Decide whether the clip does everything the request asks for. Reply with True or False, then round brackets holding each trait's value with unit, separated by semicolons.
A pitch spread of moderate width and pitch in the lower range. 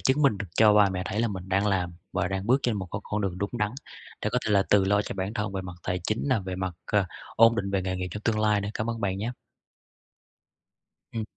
False (2.3 semitones; 100 Hz)